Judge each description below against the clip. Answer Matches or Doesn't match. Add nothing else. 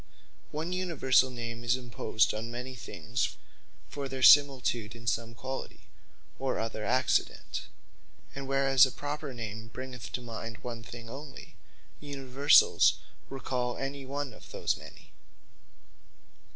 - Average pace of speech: Doesn't match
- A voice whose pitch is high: Doesn't match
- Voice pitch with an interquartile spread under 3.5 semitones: Matches